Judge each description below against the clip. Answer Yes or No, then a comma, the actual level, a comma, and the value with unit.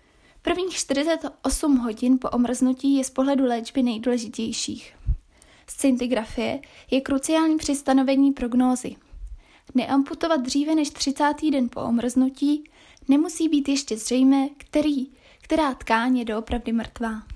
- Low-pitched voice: No, very high, 270 Hz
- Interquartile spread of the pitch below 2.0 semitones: No, average, 2.9 semitones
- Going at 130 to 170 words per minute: No, slow, 115 wpm